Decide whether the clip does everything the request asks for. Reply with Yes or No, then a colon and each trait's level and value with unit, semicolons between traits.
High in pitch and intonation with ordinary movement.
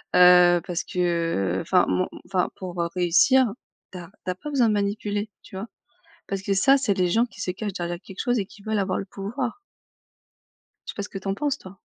Yes: high, 195 Hz; average, 3.1 semitones